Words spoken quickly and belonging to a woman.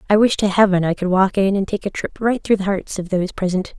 Yes: fast, 300 wpm; female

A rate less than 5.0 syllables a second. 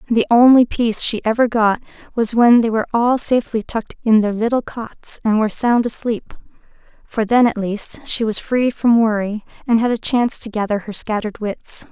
No: 5.2 syllables/s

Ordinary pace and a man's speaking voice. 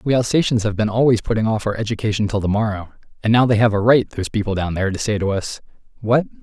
No: fast, 250 wpm; male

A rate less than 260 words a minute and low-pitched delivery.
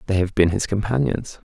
Yes: average, 200 wpm; low, 100 Hz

